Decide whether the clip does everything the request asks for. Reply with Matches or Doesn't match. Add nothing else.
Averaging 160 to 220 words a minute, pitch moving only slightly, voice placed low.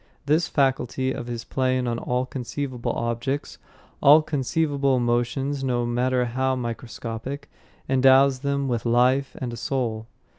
Doesn't match